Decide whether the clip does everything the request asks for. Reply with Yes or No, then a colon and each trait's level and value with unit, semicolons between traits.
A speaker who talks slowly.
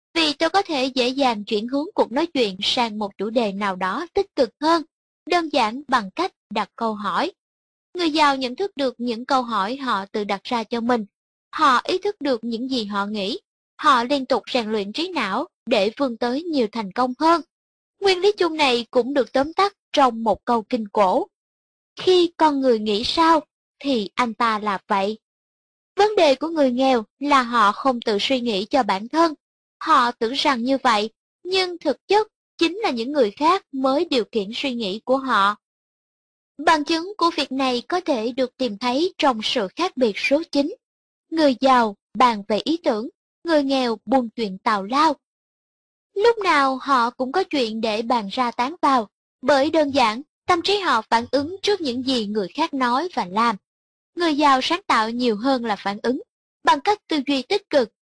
No: average, 195 wpm